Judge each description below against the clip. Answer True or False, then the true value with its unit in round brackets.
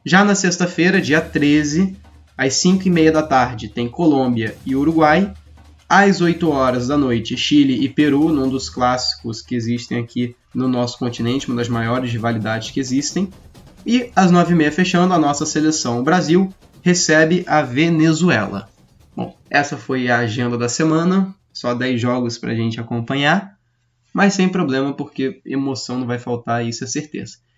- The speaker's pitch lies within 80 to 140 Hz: True (135 Hz)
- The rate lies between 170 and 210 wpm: False (160 wpm)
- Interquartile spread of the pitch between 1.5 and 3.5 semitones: False (5.6 semitones)